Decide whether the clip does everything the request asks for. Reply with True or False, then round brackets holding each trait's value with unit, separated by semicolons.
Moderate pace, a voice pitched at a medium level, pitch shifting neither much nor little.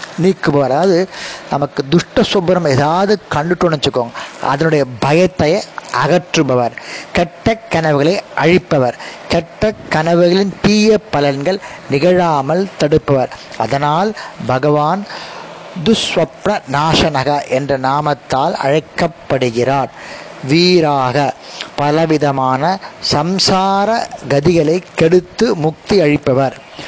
False (60 wpm; 160 Hz; 4.5 semitones)